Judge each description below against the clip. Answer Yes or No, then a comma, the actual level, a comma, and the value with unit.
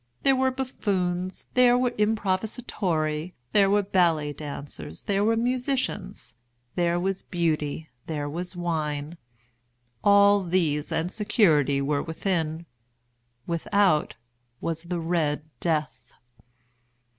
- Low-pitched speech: No, medium, 175 Hz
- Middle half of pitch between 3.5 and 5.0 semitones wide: Yes, average, 4.7 semitones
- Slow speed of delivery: Yes, slow, 105 wpm